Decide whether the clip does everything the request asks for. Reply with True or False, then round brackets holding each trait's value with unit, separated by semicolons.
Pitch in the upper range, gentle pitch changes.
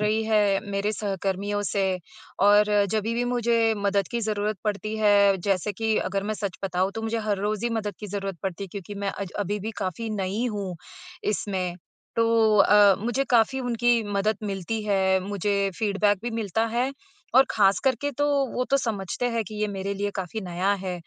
True (205 Hz; 2.2 semitones)